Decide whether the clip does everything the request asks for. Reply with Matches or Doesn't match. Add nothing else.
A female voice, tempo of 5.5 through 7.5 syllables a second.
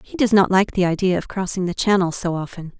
Matches